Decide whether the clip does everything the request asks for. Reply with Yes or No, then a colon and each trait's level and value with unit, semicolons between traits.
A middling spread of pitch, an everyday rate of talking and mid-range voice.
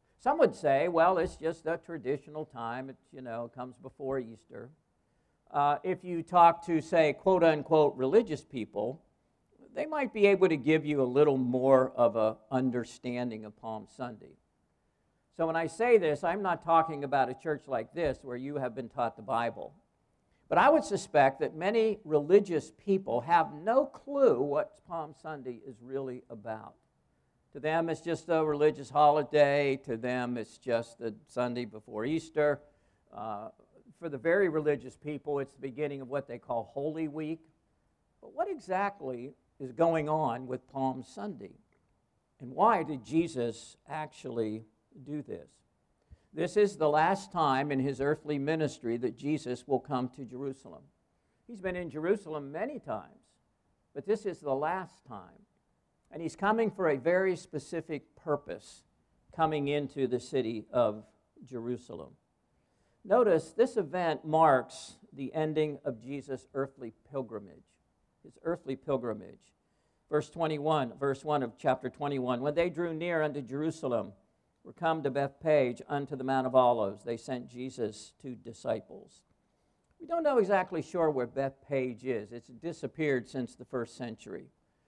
Yes: average, 4.3 semitones; average, 155 wpm; medium, 145 Hz